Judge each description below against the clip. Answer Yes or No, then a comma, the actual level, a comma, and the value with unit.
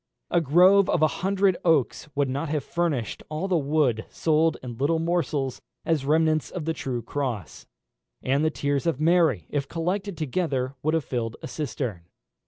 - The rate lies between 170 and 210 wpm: Yes, average, 175 wpm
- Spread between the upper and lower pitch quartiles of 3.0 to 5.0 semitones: Yes, average, 3.7 semitones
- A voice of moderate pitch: Yes, medium, 155 Hz